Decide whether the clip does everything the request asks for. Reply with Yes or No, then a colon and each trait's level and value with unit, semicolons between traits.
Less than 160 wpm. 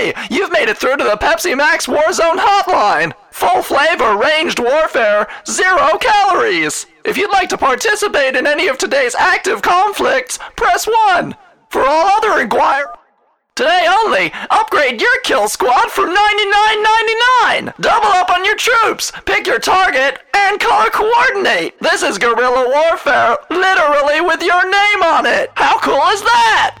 Yes: average, 150 wpm